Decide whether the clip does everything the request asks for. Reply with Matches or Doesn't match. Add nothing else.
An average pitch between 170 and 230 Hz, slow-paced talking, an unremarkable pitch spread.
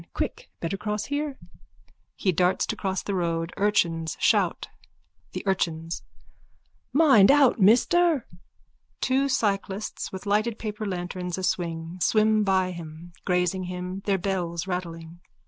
Matches